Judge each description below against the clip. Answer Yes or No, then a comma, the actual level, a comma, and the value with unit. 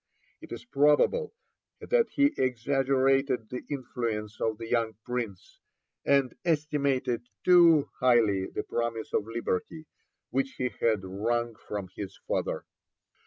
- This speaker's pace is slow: Yes, slow, 120 wpm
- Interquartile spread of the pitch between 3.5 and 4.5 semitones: Yes, average, 3.9 semitones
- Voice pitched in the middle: No, low, 125 Hz